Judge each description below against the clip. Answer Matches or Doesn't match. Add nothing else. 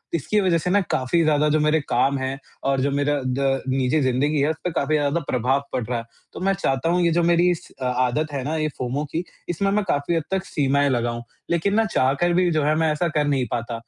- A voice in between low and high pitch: Matches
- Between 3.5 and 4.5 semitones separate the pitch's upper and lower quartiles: Matches